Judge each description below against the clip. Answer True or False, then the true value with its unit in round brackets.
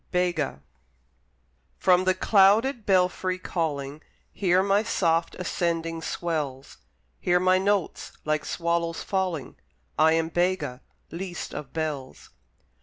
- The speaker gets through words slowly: True (110 wpm)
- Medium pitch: True (175 Hz)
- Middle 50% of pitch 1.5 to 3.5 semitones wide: True (2.7 semitones)